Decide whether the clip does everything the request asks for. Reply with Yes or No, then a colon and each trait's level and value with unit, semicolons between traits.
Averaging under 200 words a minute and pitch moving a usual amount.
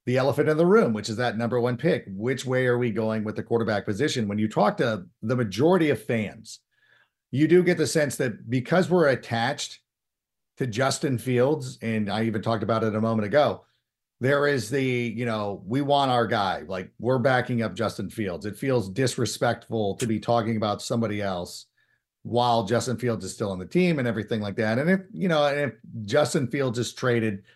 No: fast, 205 wpm; average, 3.5 semitones